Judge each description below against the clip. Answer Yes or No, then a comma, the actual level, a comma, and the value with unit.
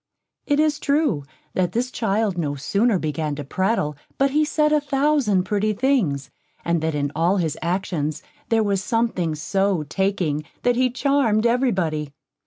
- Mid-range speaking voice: No, high, 195 Hz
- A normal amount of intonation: No, wide, 7.9 semitones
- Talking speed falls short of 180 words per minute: Yes, average, 165 wpm